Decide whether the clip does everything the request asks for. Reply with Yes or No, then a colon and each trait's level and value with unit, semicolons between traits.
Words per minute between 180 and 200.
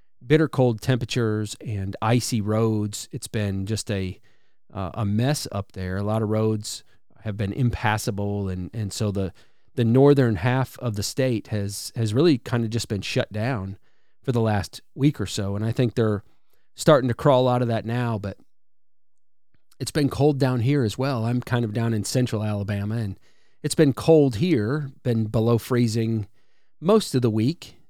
Yes: average, 185 wpm